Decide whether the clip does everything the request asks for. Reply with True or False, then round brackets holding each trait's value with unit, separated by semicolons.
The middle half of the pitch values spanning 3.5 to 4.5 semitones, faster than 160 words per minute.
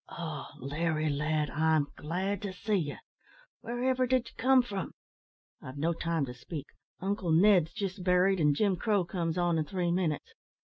True (4.1 semitones; 170 wpm)